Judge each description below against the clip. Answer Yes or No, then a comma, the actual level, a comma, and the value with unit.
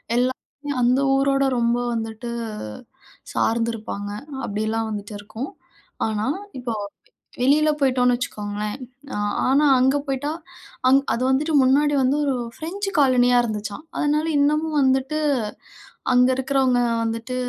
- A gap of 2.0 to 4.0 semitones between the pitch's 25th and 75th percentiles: Yes, average, 3.5 semitones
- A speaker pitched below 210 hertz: No, very high, 255 Hz